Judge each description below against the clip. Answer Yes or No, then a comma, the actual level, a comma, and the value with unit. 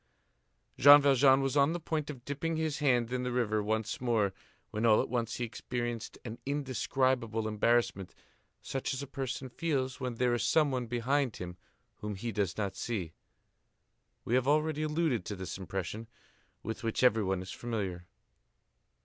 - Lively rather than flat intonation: No, average, 4.1 semitones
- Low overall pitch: Yes, low, 120 Hz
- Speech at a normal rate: Yes, average, 165 wpm